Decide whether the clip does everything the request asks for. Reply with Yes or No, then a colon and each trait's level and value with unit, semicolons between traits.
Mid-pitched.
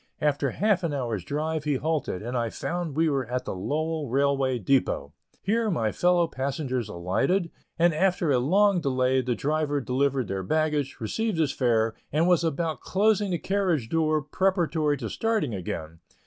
Yes: medium, 145 Hz